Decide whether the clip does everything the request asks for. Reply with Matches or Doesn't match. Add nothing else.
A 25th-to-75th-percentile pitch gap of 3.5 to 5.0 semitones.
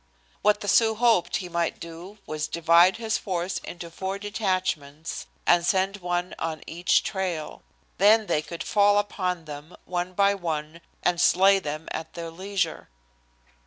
Doesn't match